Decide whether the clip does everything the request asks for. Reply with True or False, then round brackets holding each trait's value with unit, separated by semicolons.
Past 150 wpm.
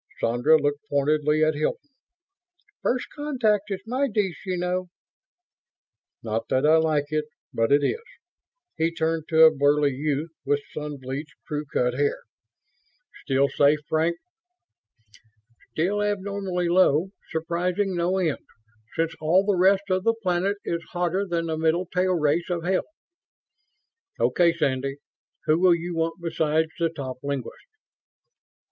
False (140 wpm)